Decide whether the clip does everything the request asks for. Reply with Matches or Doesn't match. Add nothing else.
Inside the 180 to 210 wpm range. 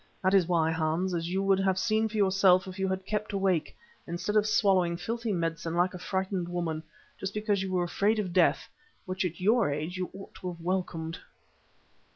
Matches